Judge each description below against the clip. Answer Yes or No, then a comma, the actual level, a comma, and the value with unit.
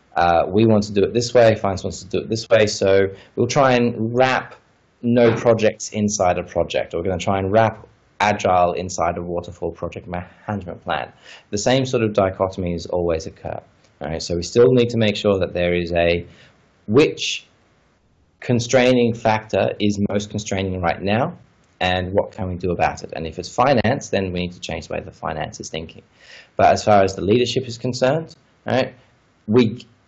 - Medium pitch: No, low, 105 Hz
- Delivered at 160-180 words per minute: No, average, 200 wpm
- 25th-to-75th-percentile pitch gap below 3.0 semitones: No, average, 4.4 semitones